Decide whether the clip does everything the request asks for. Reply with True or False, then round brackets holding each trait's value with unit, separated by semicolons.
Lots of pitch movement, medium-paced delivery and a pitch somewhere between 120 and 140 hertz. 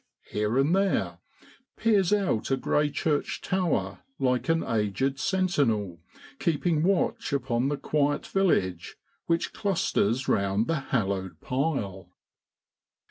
False (7.8 semitones; 115 wpm; 135 Hz)